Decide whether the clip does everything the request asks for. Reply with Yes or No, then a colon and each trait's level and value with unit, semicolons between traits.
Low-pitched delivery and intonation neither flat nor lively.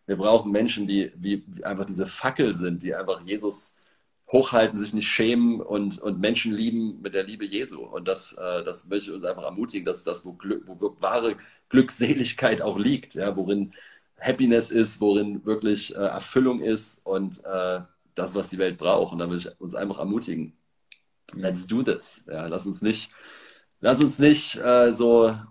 Yes: low, 105 Hz; average, 3.3 semitones